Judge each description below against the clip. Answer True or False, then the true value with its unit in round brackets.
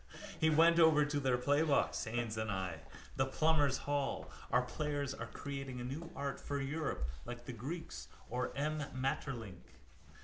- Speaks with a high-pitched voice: False (135 Hz)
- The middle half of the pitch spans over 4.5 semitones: False (3.5 semitones)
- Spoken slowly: False (160 wpm)